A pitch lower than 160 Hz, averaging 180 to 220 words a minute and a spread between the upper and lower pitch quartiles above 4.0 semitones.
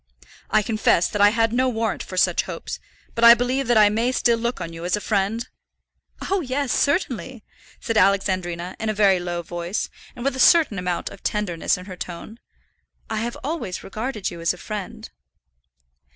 No: high, 215 Hz; average, 190 wpm; average, 4.7 semitones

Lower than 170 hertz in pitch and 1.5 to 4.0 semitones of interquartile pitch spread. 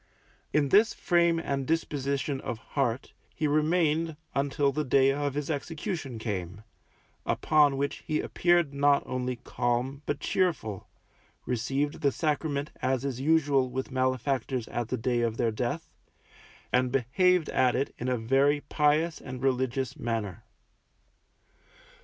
Yes: medium, 140 Hz; average, 3.2 semitones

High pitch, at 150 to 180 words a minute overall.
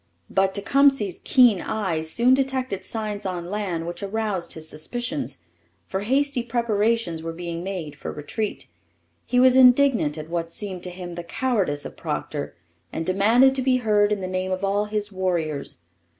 Yes: high, 200 Hz; average, 165 wpm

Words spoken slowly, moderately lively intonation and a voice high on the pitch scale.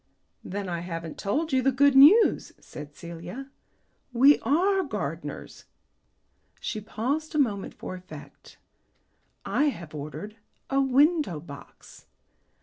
No: slow, 120 wpm; wide, 8.5 semitones; high, 245 Hz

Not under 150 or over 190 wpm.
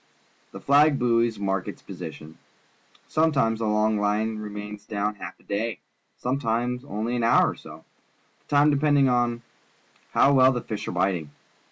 Yes: average, 160 wpm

